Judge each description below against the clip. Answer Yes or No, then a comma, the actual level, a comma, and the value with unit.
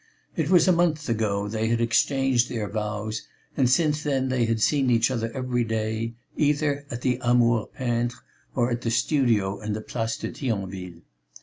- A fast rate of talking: No, average, 180 wpm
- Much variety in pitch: No, average, 3.3 semitones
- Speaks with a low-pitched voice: Yes, low, 120 Hz